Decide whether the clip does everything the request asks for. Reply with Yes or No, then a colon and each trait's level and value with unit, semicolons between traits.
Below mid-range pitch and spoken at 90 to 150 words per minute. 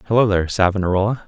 Yes: low, 100 Hz; average, 140 wpm